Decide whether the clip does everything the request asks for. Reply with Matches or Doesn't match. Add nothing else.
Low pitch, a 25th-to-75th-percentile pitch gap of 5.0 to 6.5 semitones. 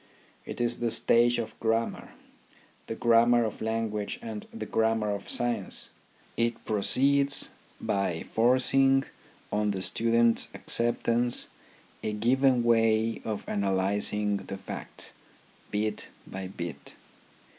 Doesn't match